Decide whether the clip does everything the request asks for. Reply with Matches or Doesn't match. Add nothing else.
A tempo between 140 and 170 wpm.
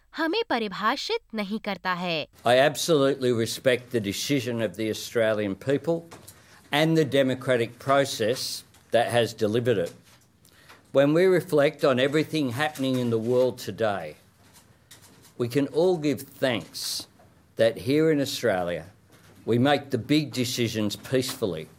Doesn't match